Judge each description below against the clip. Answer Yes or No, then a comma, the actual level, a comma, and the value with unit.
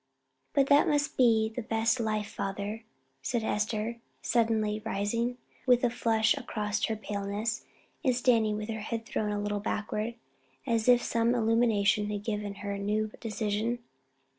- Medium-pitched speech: No, high, 220 Hz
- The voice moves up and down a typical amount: No, narrow, 1.9 semitones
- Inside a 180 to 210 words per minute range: No, average, 155 wpm